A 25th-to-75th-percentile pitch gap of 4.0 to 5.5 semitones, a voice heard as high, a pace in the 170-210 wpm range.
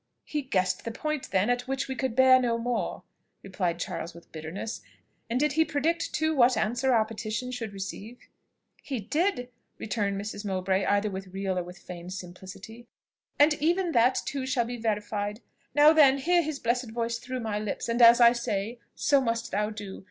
Yes: average, 4.6 semitones; high, 230 Hz; average, 190 wpm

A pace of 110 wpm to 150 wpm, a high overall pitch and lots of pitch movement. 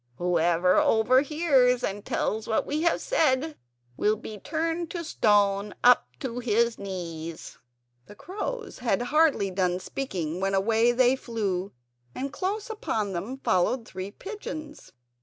Yes: slow, 135 wpm; high, 230 Hz; wide, 7.2 semitones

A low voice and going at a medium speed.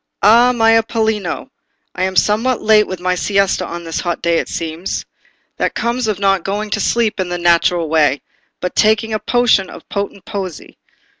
No: high, 200 Hz; average, 180 wpm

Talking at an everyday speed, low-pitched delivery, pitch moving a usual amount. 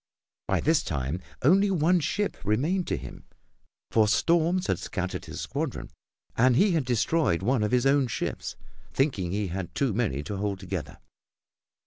No: average, 160 wpm; low, 125 Hz; wide, 8.7 semitones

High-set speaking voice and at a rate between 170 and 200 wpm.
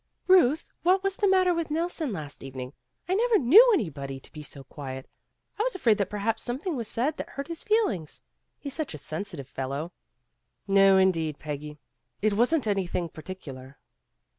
Yes: high, 205 Hz; average, 175 wpm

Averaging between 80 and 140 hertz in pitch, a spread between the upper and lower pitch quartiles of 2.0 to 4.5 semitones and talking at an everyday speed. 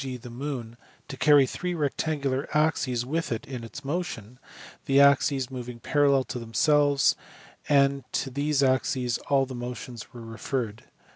Yes: low, 135 Hz; average, 2.7 semitones; average, 150 wpm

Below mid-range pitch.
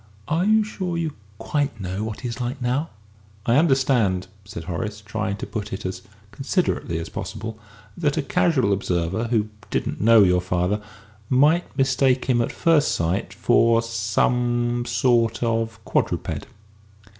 Yes: low, 115 Hz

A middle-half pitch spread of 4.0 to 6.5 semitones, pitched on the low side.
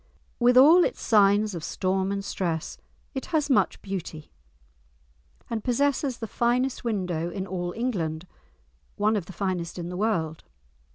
No: average, 5.3 semitones; high, 200 Hz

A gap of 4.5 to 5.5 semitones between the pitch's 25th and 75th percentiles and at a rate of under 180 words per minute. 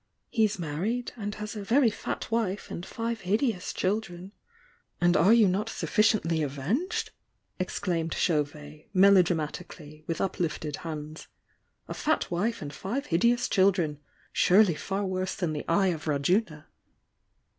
Yes: average, 5.1 semitones; average, 140 wpm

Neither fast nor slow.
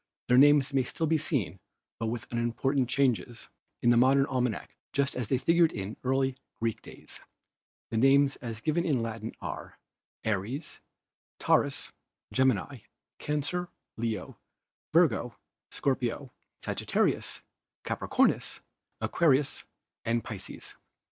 No: slow, 120 wpm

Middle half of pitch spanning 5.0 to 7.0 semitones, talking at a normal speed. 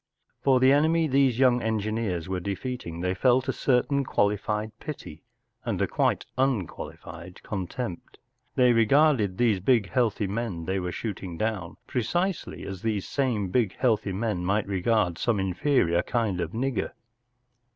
Yes: average, 5.3 semitones; average, 145 wpm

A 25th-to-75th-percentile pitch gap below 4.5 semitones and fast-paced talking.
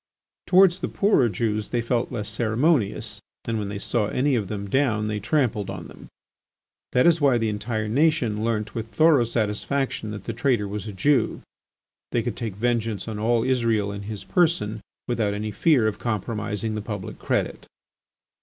No: average, 3.1 semitones; average, 175 wpm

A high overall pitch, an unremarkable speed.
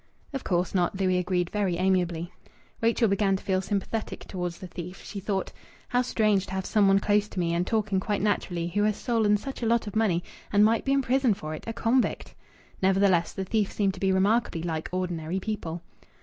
No: high, 195 Hz; fast, 210 wpm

